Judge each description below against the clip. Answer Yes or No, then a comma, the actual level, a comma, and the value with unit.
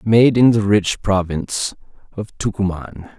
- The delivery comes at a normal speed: No, slow, 130 wpm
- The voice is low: Yes, low, 105 Hz